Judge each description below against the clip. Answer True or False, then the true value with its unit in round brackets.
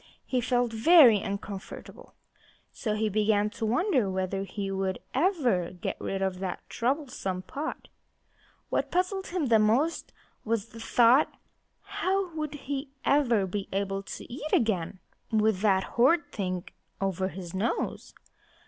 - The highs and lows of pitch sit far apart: True (6.2 semitones)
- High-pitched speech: True (220 Hz)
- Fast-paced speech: False (135 wpm)